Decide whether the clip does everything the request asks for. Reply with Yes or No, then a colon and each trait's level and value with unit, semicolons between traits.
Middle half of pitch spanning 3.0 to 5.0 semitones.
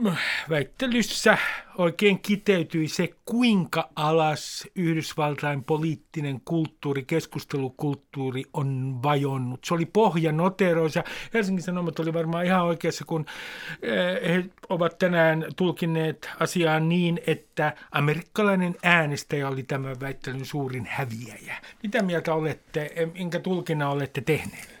Yes: average, 3.3 semitones